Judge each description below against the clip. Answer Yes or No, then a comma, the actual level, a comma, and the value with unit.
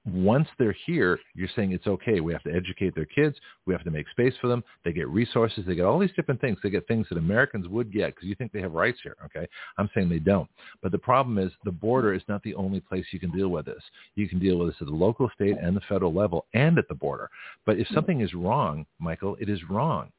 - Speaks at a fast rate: Yes, fast, 265 wpm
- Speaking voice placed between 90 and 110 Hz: Yes, low, 100 Hz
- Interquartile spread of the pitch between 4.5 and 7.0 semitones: No, average, 3.7 semitones